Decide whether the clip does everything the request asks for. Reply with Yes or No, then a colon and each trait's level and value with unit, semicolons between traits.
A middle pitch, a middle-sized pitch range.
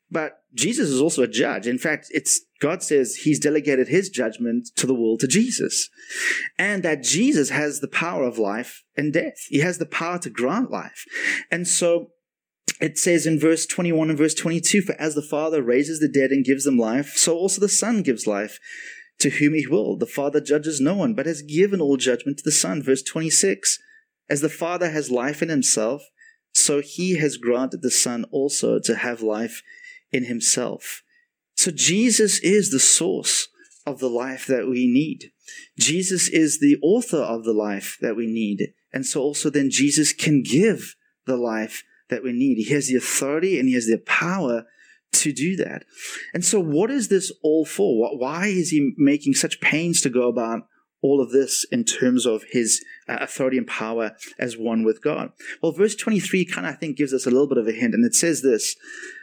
No: medium, 155 Hz; wide, 7.6 semitones